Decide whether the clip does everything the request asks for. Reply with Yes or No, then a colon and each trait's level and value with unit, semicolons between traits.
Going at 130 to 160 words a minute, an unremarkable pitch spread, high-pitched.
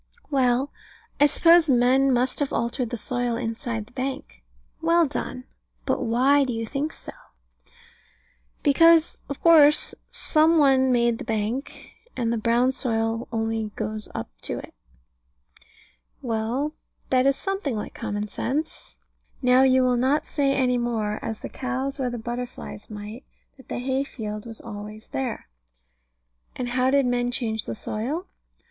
Yes: average, 150 wpm; average, 3.2 semitones; very high, 250 Hz